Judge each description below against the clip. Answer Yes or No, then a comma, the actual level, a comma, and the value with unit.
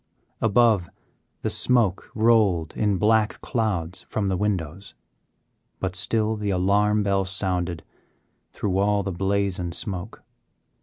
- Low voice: Yes, low, 100 Hz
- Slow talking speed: Yes, slow, 120 wpm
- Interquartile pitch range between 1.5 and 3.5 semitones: Yes, narrow, 2.6 semitones